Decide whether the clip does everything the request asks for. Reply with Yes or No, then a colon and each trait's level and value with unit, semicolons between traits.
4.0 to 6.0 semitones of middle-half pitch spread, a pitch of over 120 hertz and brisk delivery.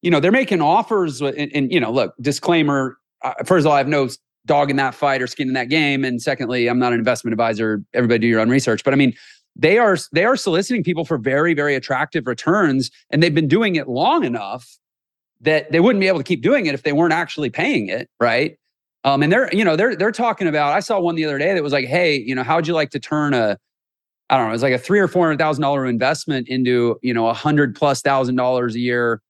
Yes: average, 4.3 semitones; medium, 140 Hz; fast, 260 wpm